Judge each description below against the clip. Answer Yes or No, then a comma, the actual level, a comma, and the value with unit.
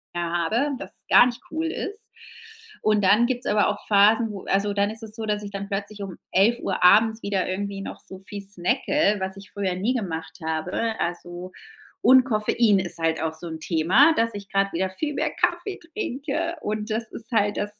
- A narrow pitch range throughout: No, average, 3.4 semitones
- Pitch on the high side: Yes, high, 205 Hz